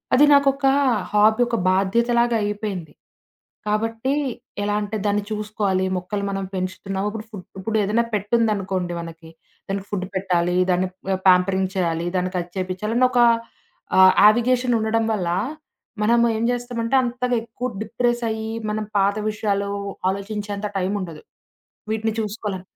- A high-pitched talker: Yes, high, 210 Hz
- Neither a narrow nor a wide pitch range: Yes, average, 3.2 semitones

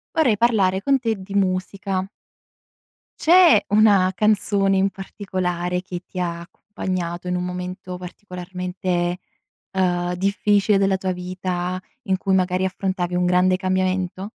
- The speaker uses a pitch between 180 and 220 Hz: Yes, medium, 185 Hz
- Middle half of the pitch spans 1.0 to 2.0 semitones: Yes, narrow, 1.6 semitones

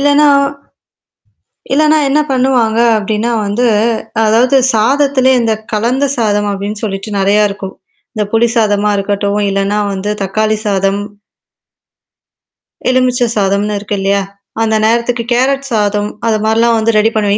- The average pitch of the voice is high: Yes, high, 215 Hz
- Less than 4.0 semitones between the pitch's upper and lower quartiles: Yes, average, 3.1 semitones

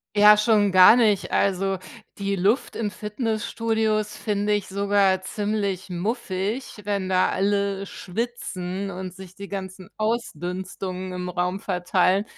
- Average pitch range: No, narrow, 2.1 semitones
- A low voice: No, high, 200 Hz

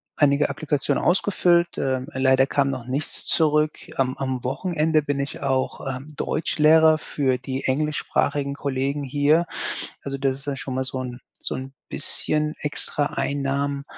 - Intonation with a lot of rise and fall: No, narrow, 2.4 semitones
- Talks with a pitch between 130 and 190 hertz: Yes, medium, 140 Hz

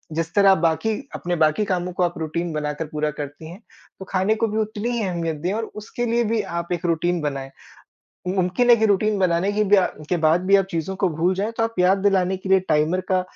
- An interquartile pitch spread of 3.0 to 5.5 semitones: Yes, average, 3.6 semitones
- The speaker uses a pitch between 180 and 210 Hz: Yes, medium, 185 Hz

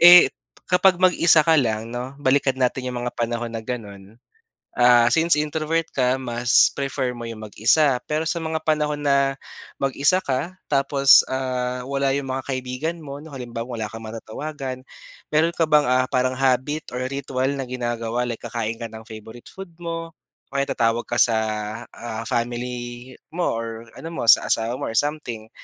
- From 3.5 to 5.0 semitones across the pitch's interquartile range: Yes, average, 4.0 semitones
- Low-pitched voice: Yes, low, 130 Hz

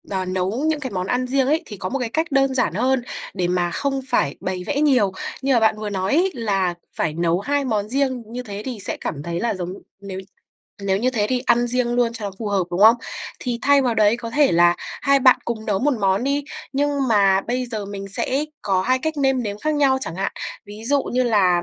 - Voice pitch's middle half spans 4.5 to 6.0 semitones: Yes, average, 5.2 semitones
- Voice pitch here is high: Yes, high, 230 Hz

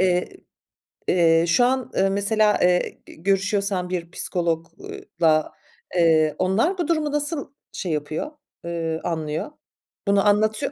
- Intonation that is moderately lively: Yes, average, 4.6 semitones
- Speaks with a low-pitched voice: No, medium, 185 Hz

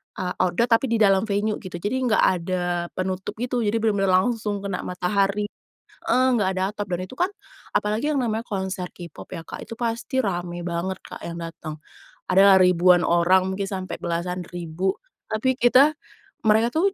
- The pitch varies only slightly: No, average, 3.8 semitones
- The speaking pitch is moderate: No, high, 195 Hz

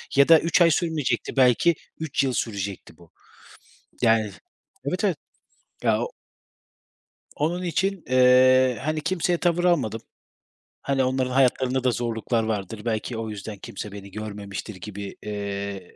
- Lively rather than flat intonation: Yes, wide, 6.3 semitones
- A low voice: Yes, low, 125 Hz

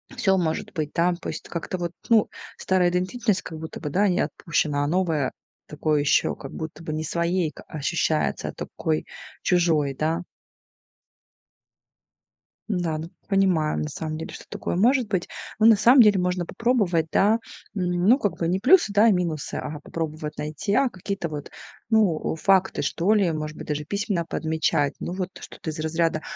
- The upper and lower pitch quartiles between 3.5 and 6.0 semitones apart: Yes, average, 3.9 semitones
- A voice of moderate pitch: Yes, medium, 170 Hz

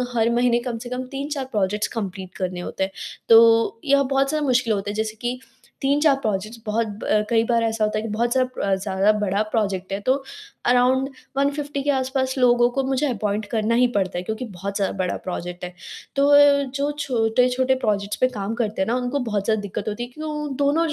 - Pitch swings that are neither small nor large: Yes, average, 4.1 semitones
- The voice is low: No, high, 230 Hz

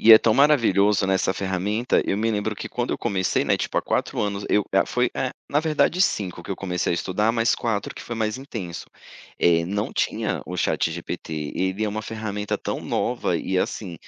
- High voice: No, low, 105 Hz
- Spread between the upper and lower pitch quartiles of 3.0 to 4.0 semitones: Yes, average, 3.3 semitones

